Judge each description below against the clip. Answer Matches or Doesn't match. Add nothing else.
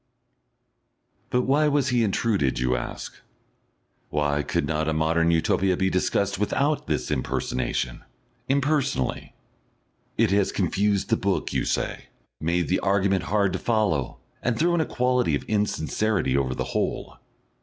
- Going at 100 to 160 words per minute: Matches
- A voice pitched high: Doesn't match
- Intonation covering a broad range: Matches